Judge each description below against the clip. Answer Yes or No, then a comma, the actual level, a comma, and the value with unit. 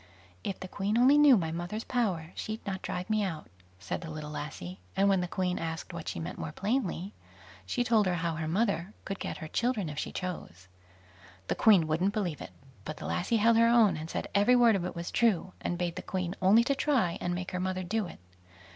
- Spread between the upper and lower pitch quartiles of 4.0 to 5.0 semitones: Yes, average, 4.6 semitones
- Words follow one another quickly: Yes, fast, 230 wpm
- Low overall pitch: No, medium, 185 Hz